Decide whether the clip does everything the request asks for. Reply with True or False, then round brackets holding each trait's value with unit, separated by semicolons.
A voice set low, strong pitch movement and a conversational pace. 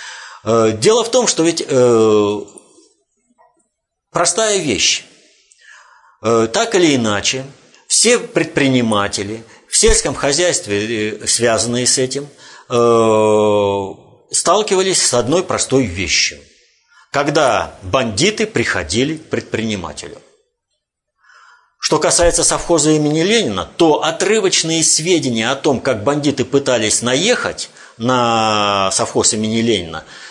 False (130 Hz; 7.7 semitones; 95 wpm)